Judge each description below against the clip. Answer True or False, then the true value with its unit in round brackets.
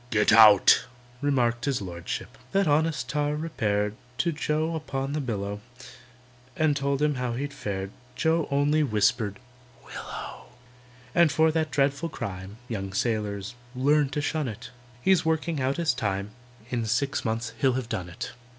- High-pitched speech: False (135 Hz)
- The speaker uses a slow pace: False (150 wpm)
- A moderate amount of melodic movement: False (5.9 semitones)